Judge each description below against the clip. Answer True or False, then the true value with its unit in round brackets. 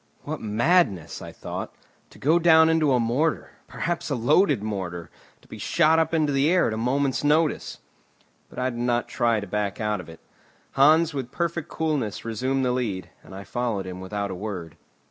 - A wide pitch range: True (6.9 semitones)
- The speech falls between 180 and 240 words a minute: True (195 wpm)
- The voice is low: True (125 Hz)